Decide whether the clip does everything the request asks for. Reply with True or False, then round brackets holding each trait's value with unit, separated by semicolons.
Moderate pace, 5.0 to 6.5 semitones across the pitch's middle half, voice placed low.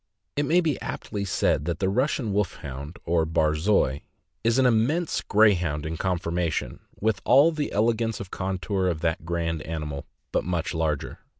True (165 wpm; 5.3 semitones; 90 Hz)